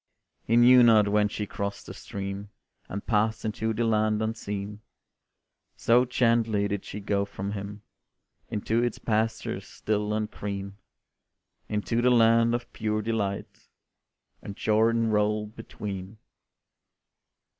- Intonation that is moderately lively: No, narrow, 1.9 semitones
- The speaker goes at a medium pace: No, slow, 125 wpm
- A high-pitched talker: No, low, 105 Hz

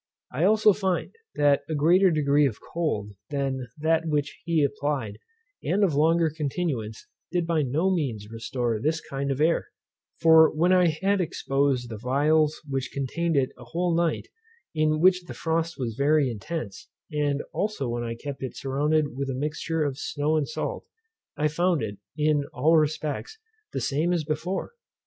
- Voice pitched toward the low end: No, medium, 150 Hz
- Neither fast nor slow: Yes, average, 170 wpm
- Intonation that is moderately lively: Yes, average, 3.4 semitones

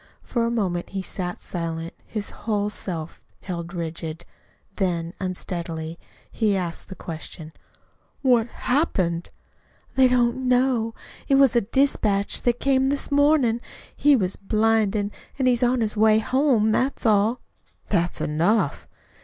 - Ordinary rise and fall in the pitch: No, wide, 5.9 semitones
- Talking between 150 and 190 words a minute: No, slow, 135 wpm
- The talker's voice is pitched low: No, high, 215 Hz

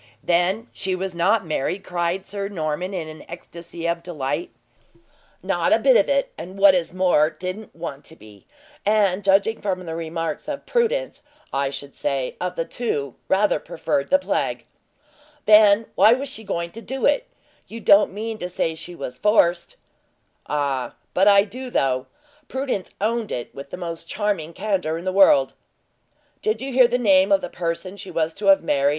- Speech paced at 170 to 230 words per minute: Yes, average, 180 wpm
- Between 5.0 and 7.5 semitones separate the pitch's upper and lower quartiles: No, average, 4.3 semitones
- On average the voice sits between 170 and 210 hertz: Yes, medium, 185 Hz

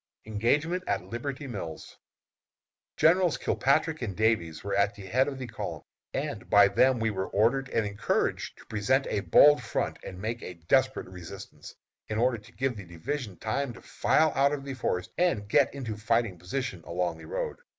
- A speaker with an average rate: Yes, average, 190 wpm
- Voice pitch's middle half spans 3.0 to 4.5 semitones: No, average, 5.3 semitones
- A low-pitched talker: Yes, low, 115 Hz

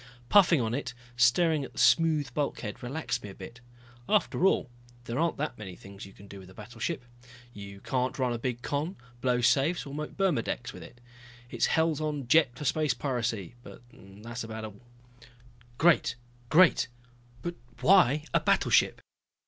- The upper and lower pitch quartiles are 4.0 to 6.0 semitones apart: Yes, average, 5.2 semitones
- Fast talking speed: No, average, 175 wpm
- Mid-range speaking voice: No, low, 125 Hz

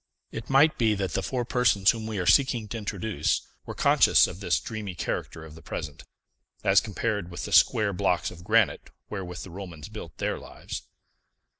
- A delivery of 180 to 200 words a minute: Yes, average, 185 wpm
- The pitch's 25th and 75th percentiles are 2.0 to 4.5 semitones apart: Yes, average, 4.0 semitones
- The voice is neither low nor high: No, low, 100 Hz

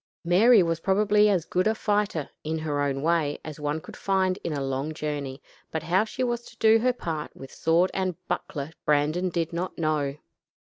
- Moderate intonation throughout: Yes, average, 4.4 semitones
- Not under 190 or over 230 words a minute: Yes, average, 195 wpm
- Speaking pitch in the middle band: Yes, medium, 165 Hz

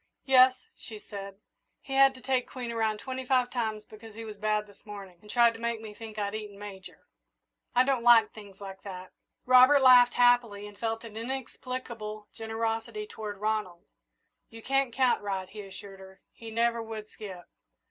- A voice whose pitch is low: No, high, 225 Hz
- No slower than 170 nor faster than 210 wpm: Yes, average, 180 wpm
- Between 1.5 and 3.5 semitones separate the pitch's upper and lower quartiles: Yes, average, 2.9 semitones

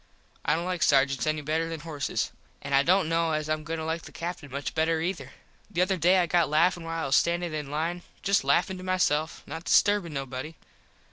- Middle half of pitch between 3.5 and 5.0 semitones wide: No, narrow, 2.6 semitones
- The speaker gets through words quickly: Yes, fast, 220 wpm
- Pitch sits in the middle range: Yes, medium, 160 Hz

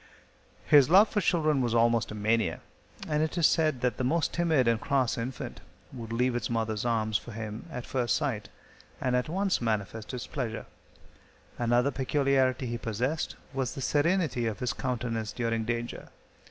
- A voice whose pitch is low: Yes, low, 125 Hz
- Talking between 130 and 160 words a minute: No, average, 170 wpm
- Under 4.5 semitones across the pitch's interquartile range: Yes, average, 3.7 semitones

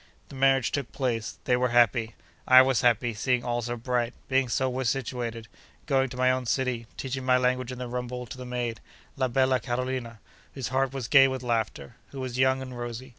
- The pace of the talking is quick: Yes, fast, 210 wpm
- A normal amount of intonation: No, narrow, 1.5 semitones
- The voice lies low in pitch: Yes, low, 125 Hz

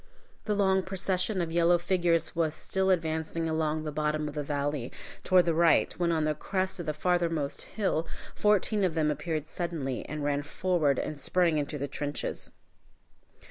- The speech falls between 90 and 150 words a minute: No, average, 175 wpm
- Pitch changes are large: No, average, 3.0 semitones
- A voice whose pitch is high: No, medium, 165 Hz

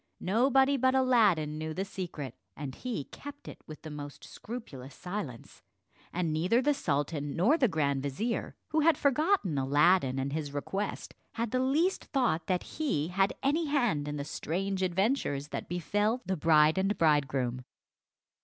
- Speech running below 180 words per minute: Yes, average, 160 wpm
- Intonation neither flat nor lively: No, wide, 9.0 semitones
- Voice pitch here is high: No, medium, 180 Hz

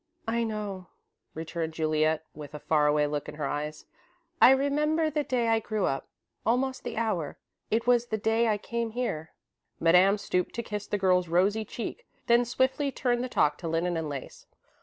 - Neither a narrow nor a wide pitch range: No, wide, 6.9 semitones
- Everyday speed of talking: Yes, average, 185 wpm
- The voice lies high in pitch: Yes, high, 210 Hz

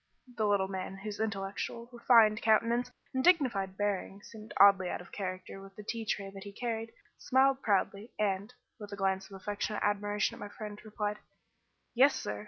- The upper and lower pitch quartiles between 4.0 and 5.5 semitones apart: No, narrow, 2.4 semitones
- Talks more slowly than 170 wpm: No, average, 180 wpm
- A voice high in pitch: Yes, high, 205 Hz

